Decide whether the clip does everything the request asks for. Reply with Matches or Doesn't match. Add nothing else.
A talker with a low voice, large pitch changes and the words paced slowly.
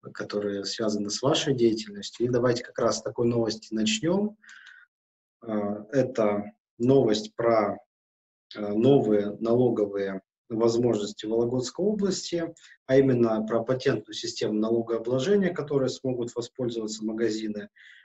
Doesn't match